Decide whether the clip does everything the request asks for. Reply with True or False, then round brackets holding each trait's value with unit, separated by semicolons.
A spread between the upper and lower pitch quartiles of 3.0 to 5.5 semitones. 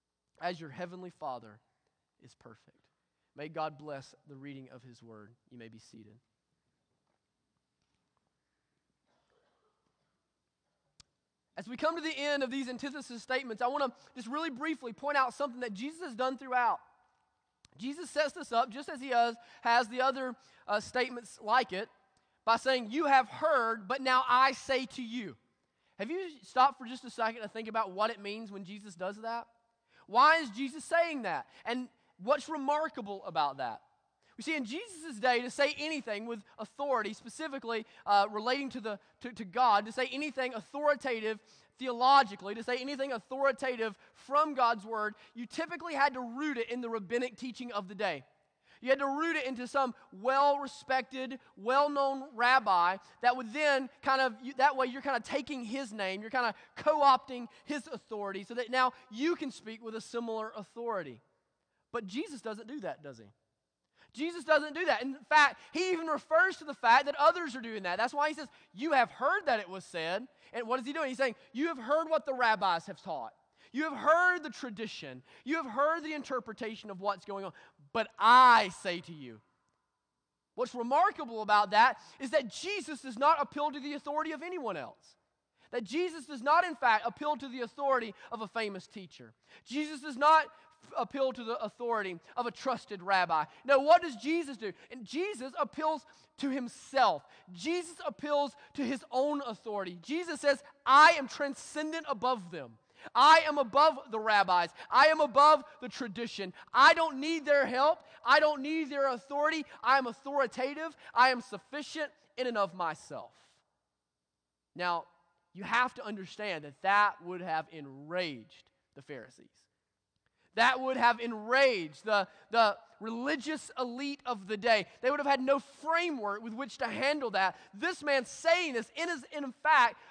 True (5.2 semitones)